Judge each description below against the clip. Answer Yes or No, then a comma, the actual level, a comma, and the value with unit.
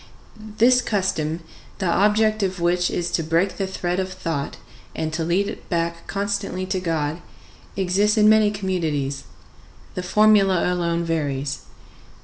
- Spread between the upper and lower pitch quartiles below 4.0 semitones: Yes, average, 3.3 semitones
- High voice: No, medium, 180 Hz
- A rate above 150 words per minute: No, average, 140 wpm